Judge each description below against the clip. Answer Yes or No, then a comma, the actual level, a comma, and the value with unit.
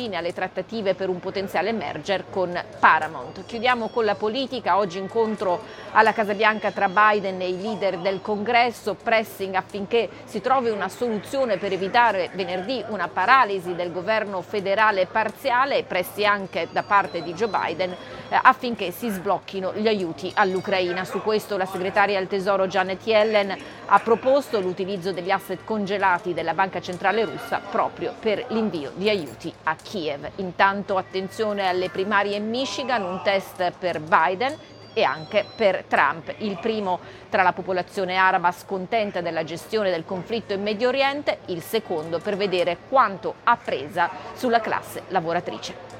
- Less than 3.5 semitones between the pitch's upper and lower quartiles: Yes, average, 2.9 semitones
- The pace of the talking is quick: No, average, 150 wpm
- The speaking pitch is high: Yes, high, 195 Hz